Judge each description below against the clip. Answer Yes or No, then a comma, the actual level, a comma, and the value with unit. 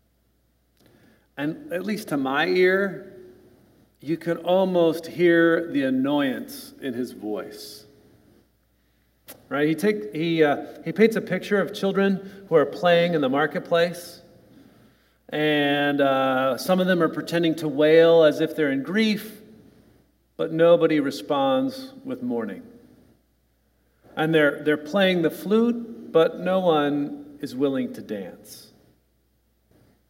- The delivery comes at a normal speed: No, slow, 130 wpm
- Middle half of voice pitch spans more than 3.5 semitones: Yes, average, 5.2 semitones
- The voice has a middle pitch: Yes, medium, 165 Hz